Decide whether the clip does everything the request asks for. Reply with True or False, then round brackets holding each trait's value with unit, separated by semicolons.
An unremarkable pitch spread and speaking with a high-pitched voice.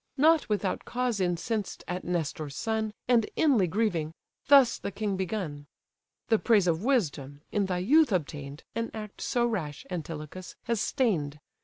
False (6.0 semitones; 195 Hz)